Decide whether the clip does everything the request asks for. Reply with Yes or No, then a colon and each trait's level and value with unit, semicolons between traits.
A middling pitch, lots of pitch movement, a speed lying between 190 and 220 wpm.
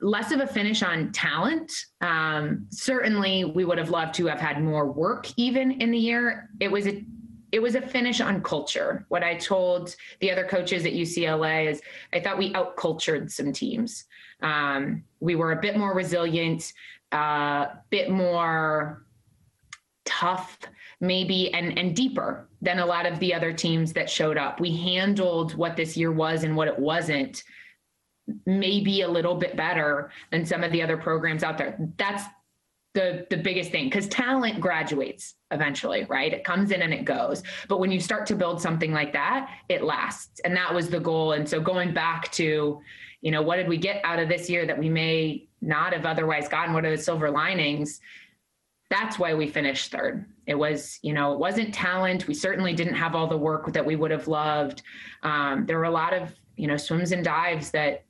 No: medium, 175 Hz; average, 3.3 semitones; average, 195 wpm